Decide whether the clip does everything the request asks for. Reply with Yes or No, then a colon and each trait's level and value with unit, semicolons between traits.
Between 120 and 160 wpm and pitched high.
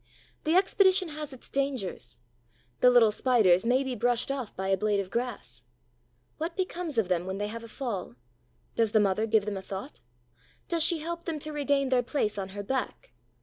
No: average, 195 wpm; high, 245 Hz